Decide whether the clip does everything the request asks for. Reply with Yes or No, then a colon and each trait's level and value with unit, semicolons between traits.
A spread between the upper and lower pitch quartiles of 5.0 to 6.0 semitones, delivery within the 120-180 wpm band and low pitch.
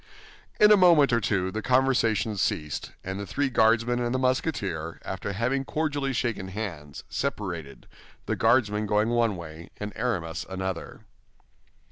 Yes: average, 5.3 semitones; average, 145 wpm; low, 110 Hz